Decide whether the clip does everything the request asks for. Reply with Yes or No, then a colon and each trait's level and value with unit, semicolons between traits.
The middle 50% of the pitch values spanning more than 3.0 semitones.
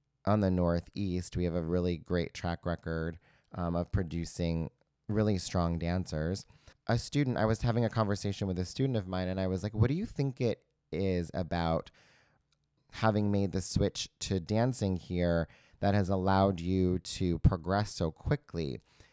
Yes: average, 3.5 semitones